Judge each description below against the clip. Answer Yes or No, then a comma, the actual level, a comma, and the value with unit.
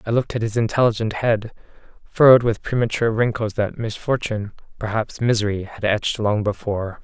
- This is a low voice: Yes, low, 110 Hz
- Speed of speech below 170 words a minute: Yes, average, 155 wpm